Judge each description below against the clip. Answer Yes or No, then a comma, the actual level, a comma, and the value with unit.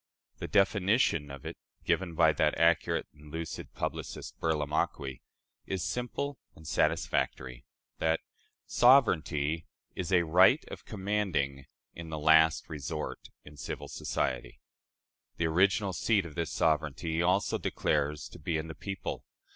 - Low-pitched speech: Yes, very low, 80 Hz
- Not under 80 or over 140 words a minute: Yes, slow, 135 wpm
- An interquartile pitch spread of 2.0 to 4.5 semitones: Yes, average, 3.9 semitones